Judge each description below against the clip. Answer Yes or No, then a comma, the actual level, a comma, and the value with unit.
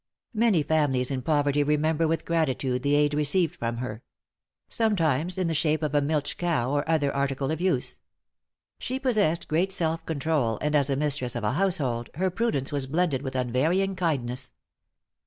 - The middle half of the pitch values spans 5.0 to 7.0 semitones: No, average, 3.7 semitones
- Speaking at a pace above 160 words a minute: Yes, average, 175 wpm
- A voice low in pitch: No, medium, 150 Hz